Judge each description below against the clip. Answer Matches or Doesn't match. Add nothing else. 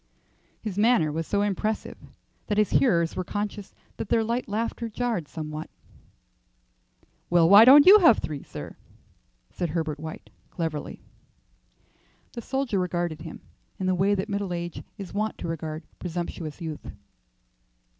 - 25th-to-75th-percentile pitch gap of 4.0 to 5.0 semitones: Matches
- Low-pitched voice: Doesn't match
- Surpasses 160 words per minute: Doesn't match